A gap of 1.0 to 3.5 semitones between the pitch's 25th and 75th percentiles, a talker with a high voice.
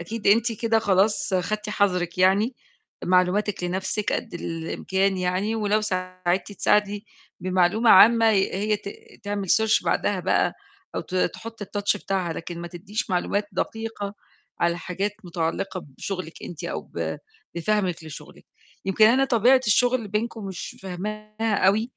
Yes: average, 2.9 semitones; high, 200 Hz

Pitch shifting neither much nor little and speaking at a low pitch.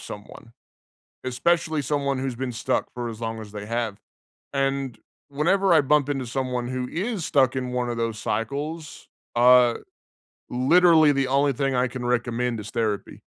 Yes: average, 3.1 semitones; low, 130 Hz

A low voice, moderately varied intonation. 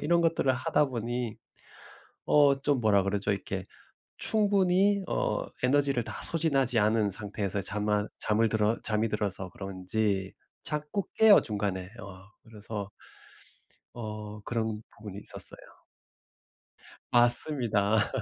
Yes: low, 110 Hz; average, 5.0 semitones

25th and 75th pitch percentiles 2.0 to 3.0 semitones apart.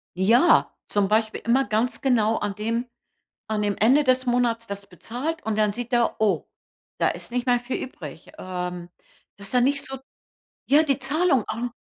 No: average, 3.5 semitones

